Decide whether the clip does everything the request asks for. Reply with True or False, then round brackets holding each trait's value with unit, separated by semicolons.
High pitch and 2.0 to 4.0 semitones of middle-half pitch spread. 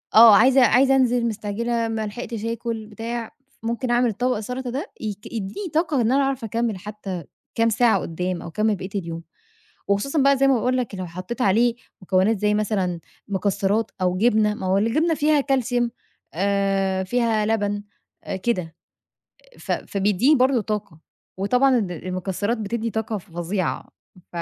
True (220 Hz; 3.6 semitones)